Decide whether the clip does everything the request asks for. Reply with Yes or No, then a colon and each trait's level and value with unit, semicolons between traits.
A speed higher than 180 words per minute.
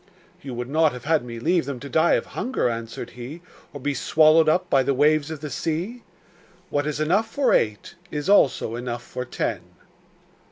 Yes: average, 195 wpm